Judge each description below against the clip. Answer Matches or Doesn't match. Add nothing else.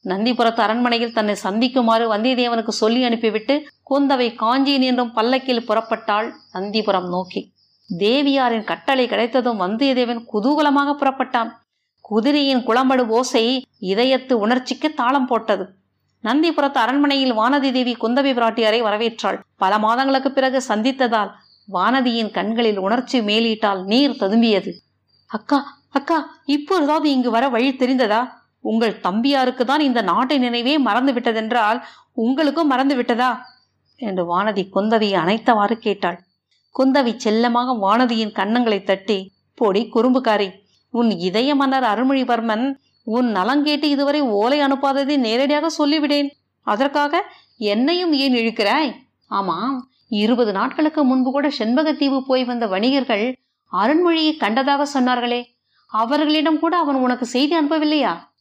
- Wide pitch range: Doesn't match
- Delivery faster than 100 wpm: Matches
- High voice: Matches